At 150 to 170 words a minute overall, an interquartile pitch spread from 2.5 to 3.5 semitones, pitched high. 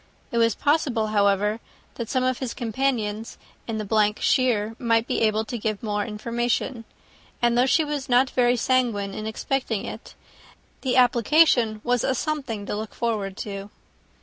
Yes: average, 160 wpm; average, 3.1 semitones; high, 230 Hz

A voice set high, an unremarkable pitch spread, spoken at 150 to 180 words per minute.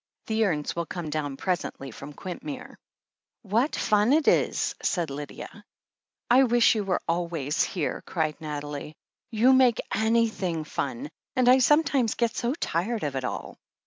No: high, 195 Hz; wide, 7.7 semitones; average, 155 wpm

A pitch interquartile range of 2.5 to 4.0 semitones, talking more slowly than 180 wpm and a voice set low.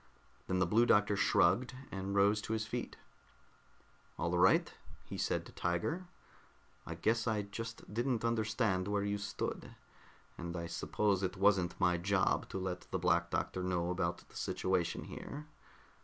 Yes: average, 3.4 semitones; average, 155 wpm; low, 100 Hz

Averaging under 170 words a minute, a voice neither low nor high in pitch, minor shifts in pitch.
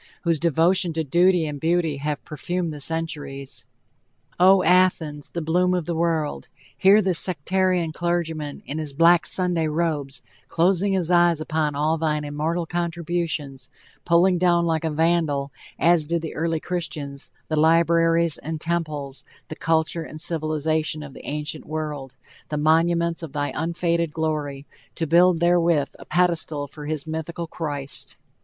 Yes: average, 150 wpm; medium, 160 Hz; narrow, 2.3 semitones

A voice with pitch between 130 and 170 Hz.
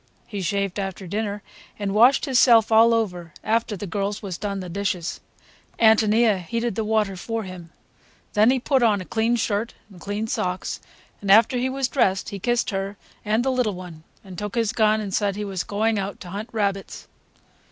No: high, 210 Hz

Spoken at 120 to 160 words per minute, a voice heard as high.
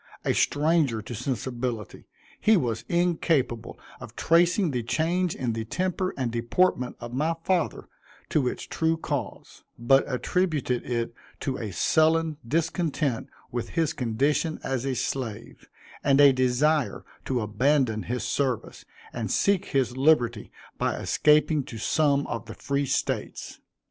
No: average, 140 wpm; low, 135 Hz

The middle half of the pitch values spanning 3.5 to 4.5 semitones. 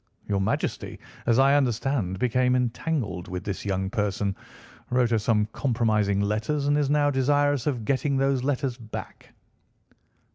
No: average, 4.9 semitones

